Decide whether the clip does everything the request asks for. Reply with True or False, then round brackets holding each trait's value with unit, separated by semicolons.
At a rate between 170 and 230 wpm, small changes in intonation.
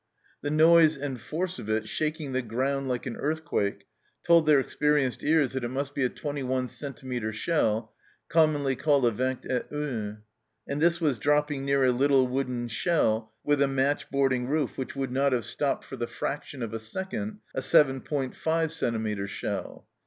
False (180 wpm; 3.1 semitones)